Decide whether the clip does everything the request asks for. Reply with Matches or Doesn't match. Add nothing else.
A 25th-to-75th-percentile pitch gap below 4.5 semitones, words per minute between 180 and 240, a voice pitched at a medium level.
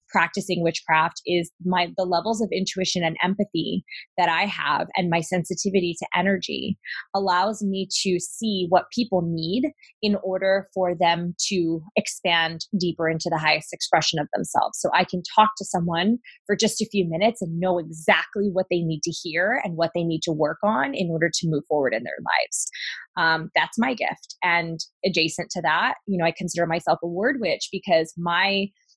Matches